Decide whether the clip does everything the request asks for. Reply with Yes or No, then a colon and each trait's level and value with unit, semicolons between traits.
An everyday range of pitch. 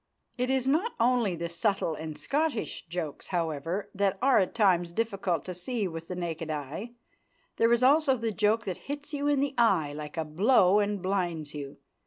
No: wide, 6.3 semitones